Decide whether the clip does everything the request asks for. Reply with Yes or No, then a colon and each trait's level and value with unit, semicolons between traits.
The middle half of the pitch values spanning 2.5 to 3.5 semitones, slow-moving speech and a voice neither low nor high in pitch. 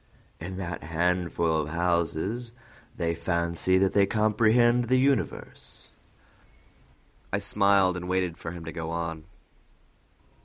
No: average, 3.2 semitones; slow, 120 wpm; very low, 90 Hz